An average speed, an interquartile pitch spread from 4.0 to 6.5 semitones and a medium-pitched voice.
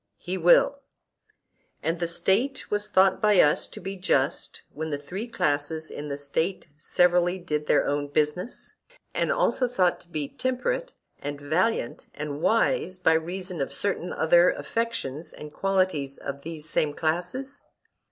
Yes: average, 150 wpm; average, 4.4 semitones; medium, 175 Hz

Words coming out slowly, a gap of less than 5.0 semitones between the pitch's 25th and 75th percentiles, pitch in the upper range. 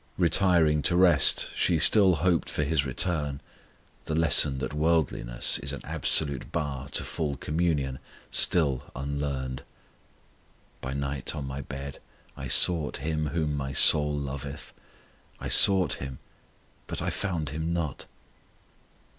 No: slow, 130 wpm; average, 3.0 semitones; very low, 75 Hz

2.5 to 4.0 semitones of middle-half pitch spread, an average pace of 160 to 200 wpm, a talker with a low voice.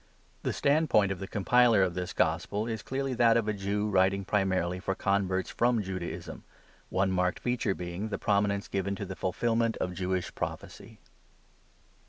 Yes: average, 3.1 semitones; average, 165 wpm; low, 100 Hz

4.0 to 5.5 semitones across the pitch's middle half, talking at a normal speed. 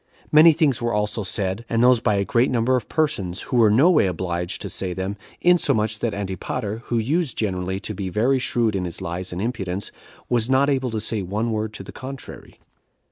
No: average, 4.7 semitones; fast, 210 wpm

